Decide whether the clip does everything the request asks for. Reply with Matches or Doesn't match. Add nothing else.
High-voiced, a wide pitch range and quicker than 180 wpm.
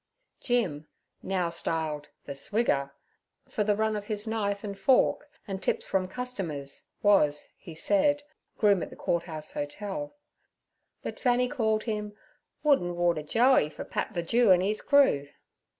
Doesn't match